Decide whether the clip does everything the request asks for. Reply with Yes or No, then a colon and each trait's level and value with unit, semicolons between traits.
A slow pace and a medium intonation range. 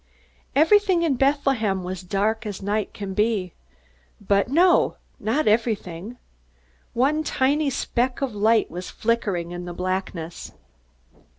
No: slow, 120 wpm; wide, 6.1 semitones